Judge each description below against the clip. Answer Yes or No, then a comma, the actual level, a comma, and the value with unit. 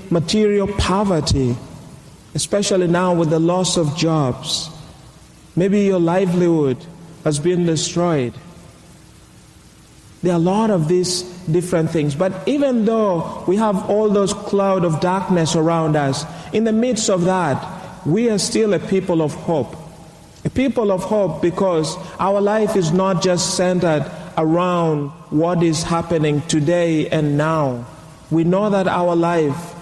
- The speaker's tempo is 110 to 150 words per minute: Yes, average, 140 wpm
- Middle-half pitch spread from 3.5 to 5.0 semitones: No, average, 3.0 semitones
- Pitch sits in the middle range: Yes, medium, 175 Hz